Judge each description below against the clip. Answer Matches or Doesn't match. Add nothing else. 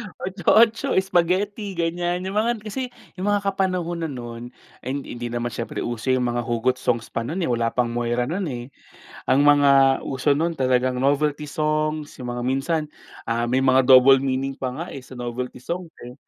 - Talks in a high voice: Doesn't match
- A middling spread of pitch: Doesn't match